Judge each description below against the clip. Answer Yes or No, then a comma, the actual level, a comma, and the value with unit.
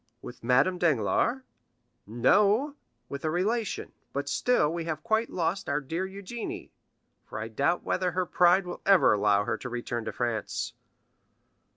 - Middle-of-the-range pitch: Yes, medium, 165 Hz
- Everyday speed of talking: Yes, average, 155 wpm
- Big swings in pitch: Yes, wide, 8.0 semitones